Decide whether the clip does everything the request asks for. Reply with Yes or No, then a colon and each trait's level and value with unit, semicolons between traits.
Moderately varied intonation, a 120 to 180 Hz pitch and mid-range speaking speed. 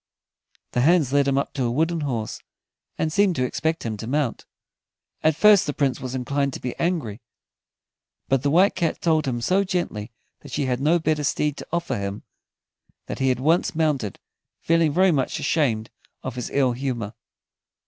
Yes: average, 4.6 semitones; medium, 140 Hz; average, 185 wpm